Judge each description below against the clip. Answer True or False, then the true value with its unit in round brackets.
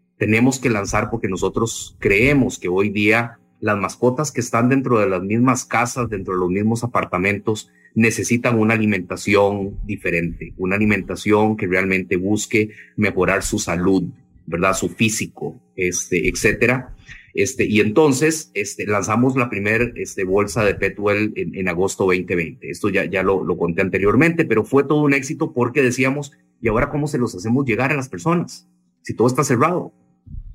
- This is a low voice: True (105 Hz)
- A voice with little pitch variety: False (4.2 semitones)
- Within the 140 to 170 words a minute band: True (165 wpm)